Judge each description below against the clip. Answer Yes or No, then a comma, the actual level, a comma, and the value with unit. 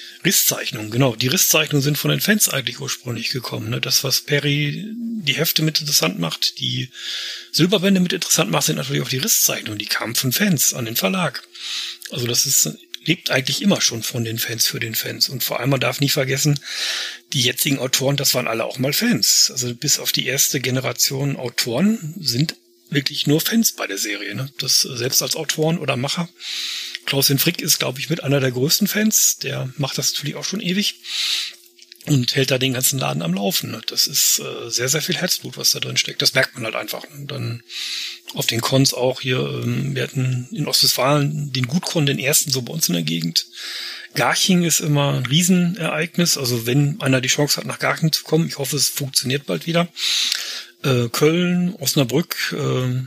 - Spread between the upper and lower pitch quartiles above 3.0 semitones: Yes, average, 3.8 semitones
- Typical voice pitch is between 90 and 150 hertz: Yes, medium, 140 Hz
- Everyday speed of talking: No, fast, 195 wpm